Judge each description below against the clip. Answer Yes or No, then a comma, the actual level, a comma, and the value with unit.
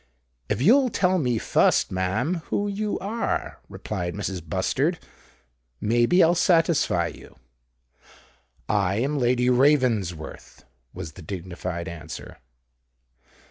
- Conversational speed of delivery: No, slow, 110 wpm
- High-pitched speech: No, low, 120 Hz